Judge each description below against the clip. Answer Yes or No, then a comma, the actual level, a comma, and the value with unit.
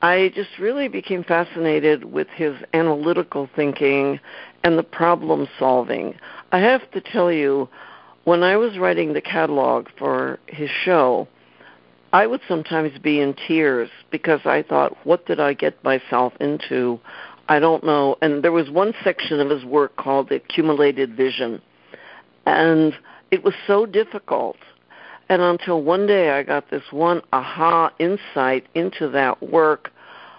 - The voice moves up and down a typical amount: Yes, average, 4.0 semitones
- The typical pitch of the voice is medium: Yes, medium, 155 Hz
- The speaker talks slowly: No, average, 145 wpm